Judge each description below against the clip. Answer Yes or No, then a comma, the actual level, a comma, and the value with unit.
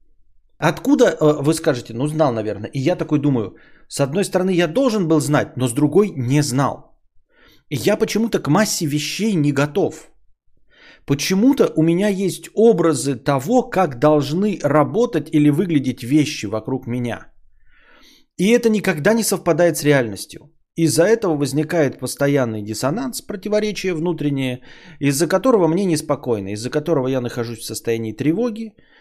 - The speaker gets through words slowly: No, average, 145 wpm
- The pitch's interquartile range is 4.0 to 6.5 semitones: Yes, wide, 5.5 semitones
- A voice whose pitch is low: No, medium, 155 Hz